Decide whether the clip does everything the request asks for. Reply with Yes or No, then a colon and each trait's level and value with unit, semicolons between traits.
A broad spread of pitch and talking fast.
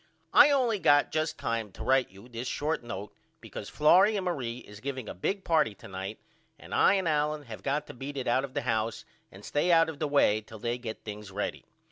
Yes: wide, 6.0 semitones; fast, 230 wpm